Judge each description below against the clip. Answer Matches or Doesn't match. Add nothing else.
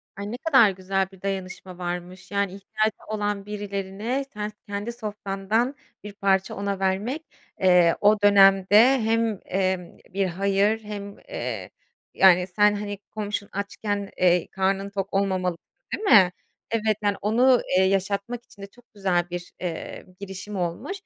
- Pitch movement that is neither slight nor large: Doesn't match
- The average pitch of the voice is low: Doesn't match